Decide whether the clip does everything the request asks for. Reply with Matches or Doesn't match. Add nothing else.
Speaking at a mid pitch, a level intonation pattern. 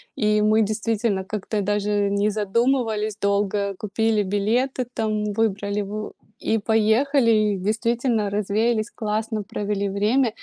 Doesn't match